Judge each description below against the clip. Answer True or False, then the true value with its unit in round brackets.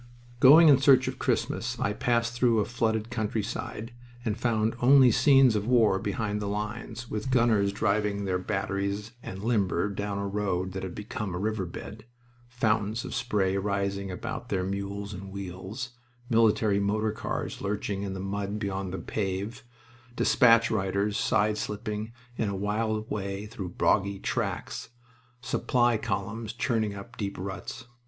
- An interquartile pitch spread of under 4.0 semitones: True (2.6 semitones)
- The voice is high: False (105 Hz)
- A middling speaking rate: True (155 wpm)